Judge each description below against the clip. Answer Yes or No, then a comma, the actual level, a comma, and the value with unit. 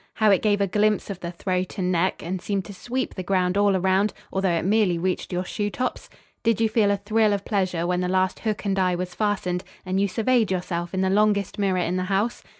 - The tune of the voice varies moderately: No, narrow, 2.2 semitones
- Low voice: No, high, 190 Hz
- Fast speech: Yes, fast, 245 wpm